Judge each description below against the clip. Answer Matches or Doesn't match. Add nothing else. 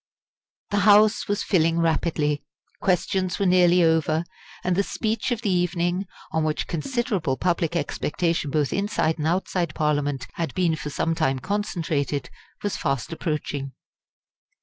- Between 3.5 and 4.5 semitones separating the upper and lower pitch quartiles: Matches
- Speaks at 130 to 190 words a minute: Matches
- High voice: Doesn't match